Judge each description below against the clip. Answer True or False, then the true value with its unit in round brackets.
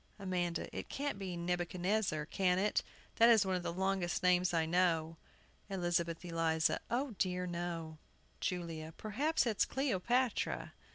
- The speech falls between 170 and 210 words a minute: False (135 wpm)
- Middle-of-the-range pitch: True (180 Hz)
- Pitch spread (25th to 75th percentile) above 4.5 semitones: False (2.7 semitones)